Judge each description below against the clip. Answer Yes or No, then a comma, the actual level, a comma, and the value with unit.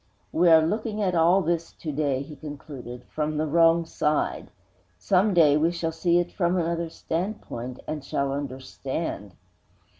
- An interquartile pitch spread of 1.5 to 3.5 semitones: Yes, average, 3.1 semitones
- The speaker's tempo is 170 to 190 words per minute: No, average, 155 wpm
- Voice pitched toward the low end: No, medium, 160 Hz